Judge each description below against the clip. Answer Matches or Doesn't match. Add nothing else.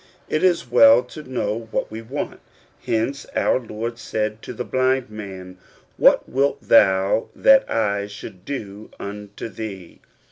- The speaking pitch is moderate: Doesn't match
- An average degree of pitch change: Matches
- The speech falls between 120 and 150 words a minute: Matches